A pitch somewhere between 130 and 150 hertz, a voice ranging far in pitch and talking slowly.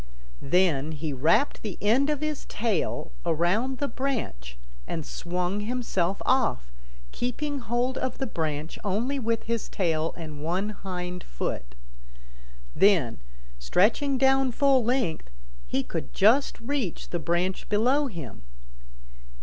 No: high, 200 Hz; wide, 7.6 semitones; slow, 125 wpm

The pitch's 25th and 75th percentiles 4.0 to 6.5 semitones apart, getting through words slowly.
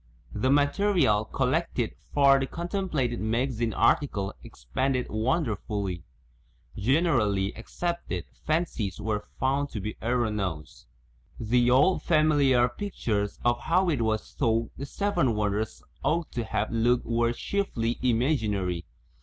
Yes: average, 5.1 semitones; slow, 120 wpm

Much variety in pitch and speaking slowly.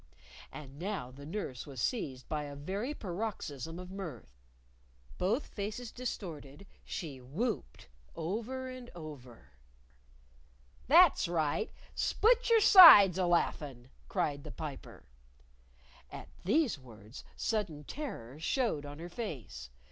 Yes: wide, 7.8 semitones; slow, 115 wpm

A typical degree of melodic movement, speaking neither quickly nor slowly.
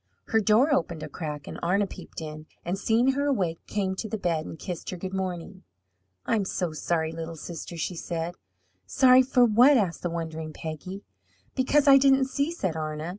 No: wide, 6.4 semitones; average, 190 wpm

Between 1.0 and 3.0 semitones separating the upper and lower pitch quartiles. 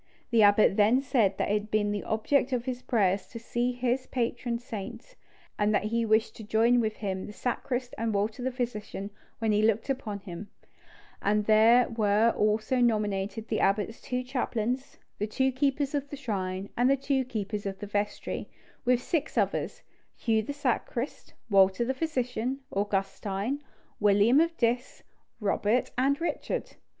No: average, 3.4 semitones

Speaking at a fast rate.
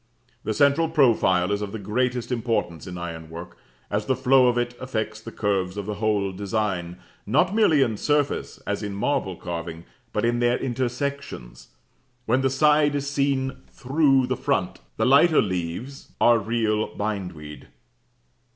No: average, 160 wpm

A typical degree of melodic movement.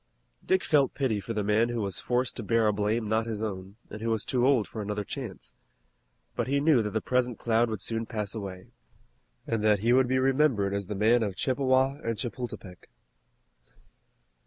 Yes: average, 3.3 semitones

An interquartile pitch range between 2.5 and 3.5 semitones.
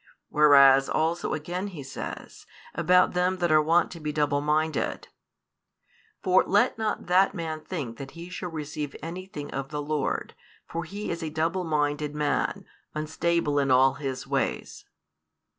Yes: average, 2.9 semitones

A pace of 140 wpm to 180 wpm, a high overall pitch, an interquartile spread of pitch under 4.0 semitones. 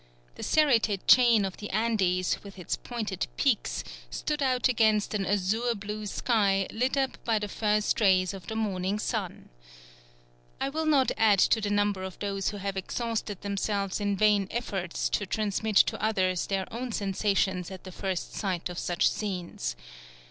Yes: average, 170 wpm; high, 205 Hz; narrow, 2.6 semitones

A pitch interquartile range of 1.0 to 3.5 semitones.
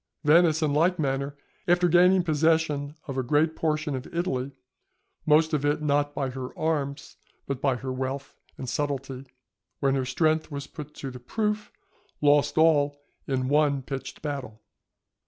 Yes: average, 2.7 semitones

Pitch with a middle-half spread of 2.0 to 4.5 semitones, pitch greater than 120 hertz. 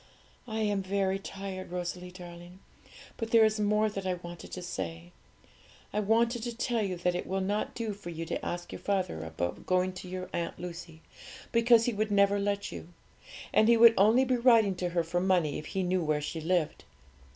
Yes: average, 3.5 semitones; high, 190 Hz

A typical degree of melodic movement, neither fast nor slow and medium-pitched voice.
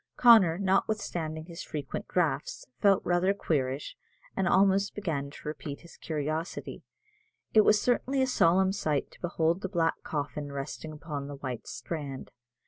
Yes: average, 4.7 semitones; average, 145 wpm; medium, 165 Hz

